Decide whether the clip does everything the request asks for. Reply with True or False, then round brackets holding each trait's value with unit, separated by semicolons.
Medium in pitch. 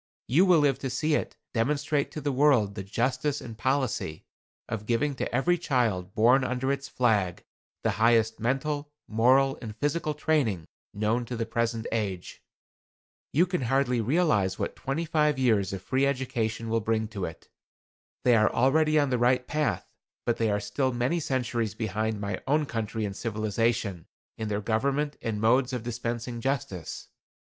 False (120 Hz)